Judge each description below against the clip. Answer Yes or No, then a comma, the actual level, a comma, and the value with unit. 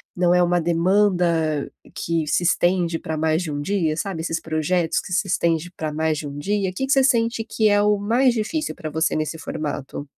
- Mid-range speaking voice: Yes, medium, 175 Hz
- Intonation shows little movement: No, average, 4.3 semitones